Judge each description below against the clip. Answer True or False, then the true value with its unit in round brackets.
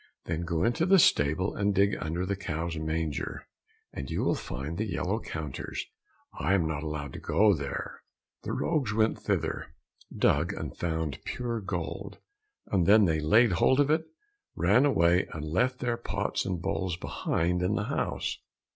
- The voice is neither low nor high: False (90 Hz)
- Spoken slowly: False (165 wpm)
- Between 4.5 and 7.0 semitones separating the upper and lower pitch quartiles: True (5.2 semitones)